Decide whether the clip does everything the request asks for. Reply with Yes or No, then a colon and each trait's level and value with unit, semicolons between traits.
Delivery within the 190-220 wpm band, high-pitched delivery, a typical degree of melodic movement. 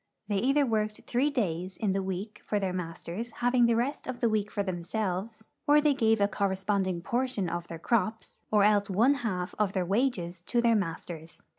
Yes: average, 200 wpm; high, 210 Hz; average, 4.2 semitones